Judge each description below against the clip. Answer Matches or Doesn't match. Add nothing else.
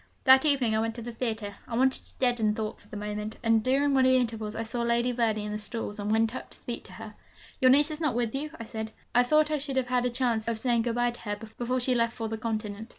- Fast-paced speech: Matches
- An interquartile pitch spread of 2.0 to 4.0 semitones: Matches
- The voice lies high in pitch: Matches